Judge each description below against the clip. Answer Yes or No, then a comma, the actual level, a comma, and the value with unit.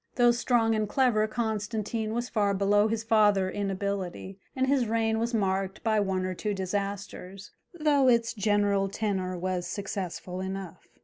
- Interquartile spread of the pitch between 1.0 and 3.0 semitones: Yes, average, 2.7 semitones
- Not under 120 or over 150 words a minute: No, average, 160 wpm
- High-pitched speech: Yes, high, 205 Hz